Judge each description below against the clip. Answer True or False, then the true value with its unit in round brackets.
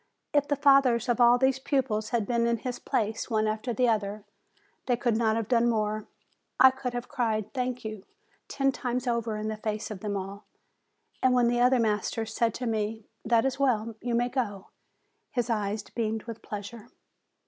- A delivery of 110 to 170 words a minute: False (190 wpm)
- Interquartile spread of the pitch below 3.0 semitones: True (2.5 semitones)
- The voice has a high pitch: True (230 Hz)